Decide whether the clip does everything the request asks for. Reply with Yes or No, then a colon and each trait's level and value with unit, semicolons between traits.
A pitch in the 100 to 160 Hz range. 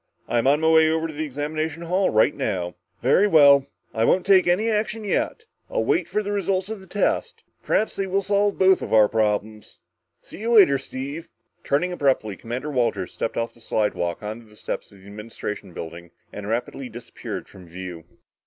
Yes: medium, 140 Hz